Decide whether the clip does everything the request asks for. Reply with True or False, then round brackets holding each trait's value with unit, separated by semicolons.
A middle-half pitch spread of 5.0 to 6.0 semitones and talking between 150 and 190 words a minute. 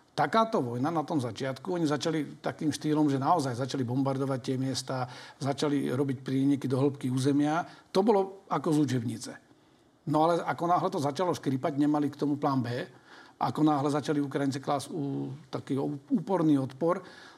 False (2.8 semitones; 160 wpm)